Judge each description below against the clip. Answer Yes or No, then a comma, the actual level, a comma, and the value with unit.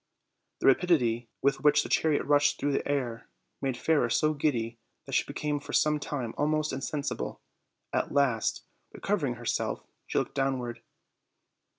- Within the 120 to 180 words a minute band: Yes, average, 150 wpm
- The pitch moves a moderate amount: Yes, average, 3.4 semitones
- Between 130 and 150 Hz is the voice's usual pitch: Yes, medium, 140 Hz